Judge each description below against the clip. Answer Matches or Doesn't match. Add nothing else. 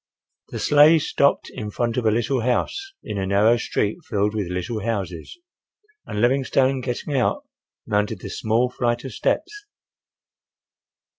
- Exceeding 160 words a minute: Doesn't match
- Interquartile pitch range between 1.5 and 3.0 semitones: Doesn't match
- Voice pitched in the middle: Doesn't match